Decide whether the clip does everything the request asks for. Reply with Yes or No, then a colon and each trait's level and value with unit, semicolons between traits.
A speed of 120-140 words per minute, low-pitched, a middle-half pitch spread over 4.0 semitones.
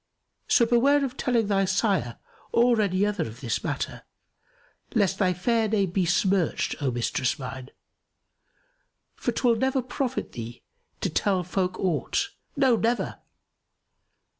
No: slow, 135 wpm; high, 200 Hz; average, 5.3 semitones